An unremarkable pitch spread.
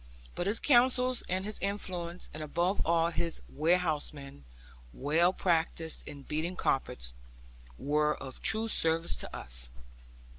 Yes: average, 3.7 semitones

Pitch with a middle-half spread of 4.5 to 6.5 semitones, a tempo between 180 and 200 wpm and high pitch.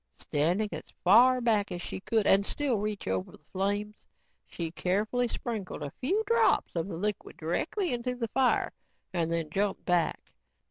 No: wide, 5.5 semitones; average, 170 wpm; high, 205 Hz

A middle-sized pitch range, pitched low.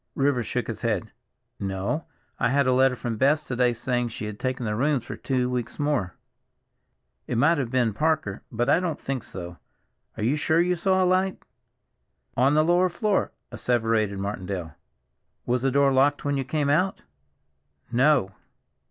Yes: average, 4.5 semitones; low, 130 Hz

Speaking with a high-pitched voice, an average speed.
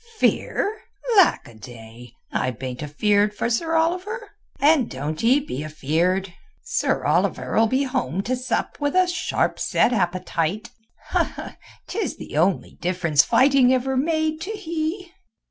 No: high, 240 Hz; slow, 125 wpm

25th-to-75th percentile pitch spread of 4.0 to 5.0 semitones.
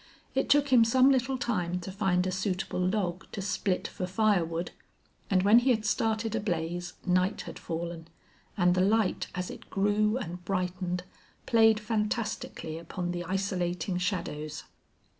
No: average, 3.4 semitones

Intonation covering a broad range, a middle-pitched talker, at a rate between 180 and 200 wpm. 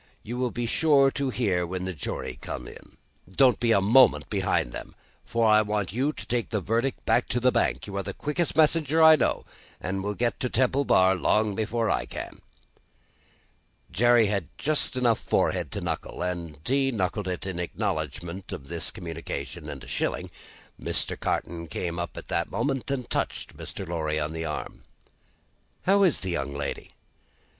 No: wide, 6.4 semitones; low, 105 Hz; average, 185 wpm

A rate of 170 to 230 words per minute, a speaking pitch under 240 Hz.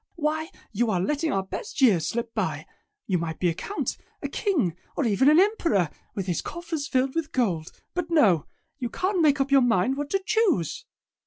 No: average, 195 wpm; very high, 260 Hz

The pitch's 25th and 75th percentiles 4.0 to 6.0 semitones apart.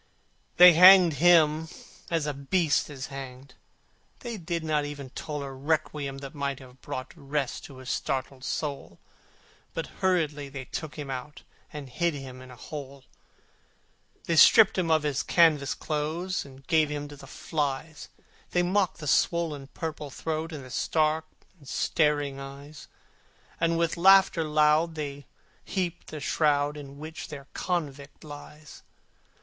No: average, 2.7 semitones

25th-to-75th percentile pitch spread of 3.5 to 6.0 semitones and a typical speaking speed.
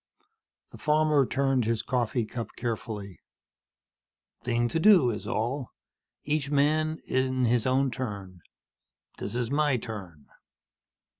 No: average, 4.0 semitones; slow, 120 wpm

